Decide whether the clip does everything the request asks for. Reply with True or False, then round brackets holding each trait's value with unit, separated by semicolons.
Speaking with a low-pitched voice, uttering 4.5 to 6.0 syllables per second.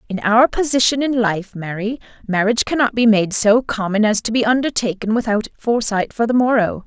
False (220 Hz; 5.5 syllables/s)